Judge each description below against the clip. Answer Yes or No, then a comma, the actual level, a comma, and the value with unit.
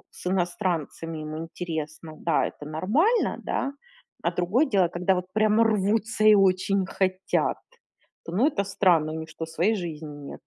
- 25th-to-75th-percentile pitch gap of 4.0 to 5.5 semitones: Yes, average, 4.3 semitones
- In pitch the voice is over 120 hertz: Yes, medium, 185 Hz